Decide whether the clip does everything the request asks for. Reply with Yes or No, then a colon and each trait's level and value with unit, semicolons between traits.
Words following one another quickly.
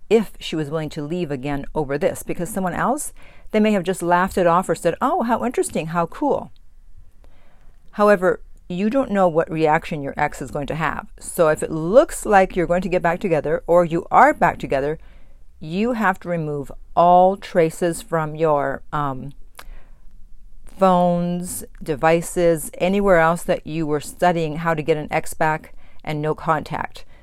No: average, 175 wpm